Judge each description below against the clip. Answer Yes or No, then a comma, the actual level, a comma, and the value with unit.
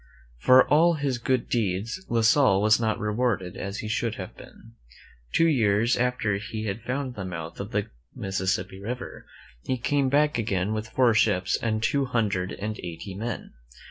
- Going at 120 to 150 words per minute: No, average, 175 wpm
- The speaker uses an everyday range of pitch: Yes, average, 4.1 semitones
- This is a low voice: Yes, low, 110 Hz